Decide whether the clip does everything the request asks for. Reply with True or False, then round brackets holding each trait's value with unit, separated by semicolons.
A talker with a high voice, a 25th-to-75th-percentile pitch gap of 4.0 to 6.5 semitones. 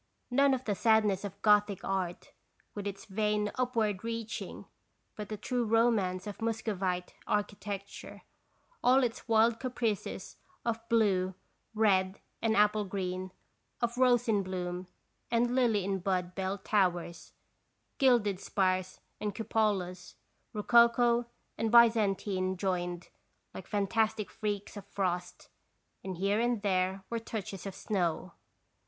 False (205 Hz; 3.2 semitones)